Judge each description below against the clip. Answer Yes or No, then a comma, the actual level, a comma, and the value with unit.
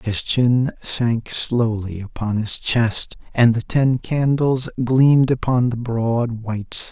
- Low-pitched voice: Yes, low, 120 Hz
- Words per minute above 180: No, average, 150 wpm